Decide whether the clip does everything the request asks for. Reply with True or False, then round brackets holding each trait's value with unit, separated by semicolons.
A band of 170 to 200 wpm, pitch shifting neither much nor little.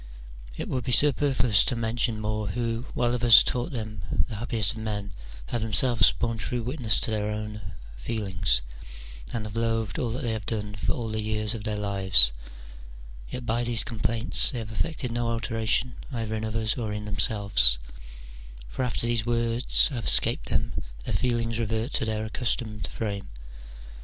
False (175 wpm; 1.9 semitones)